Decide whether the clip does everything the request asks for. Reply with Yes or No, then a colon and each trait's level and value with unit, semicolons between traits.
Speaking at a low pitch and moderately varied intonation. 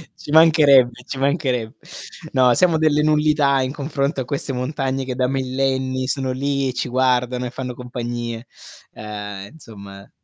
No: low, 130 Hz; narrow, 2.2 semitones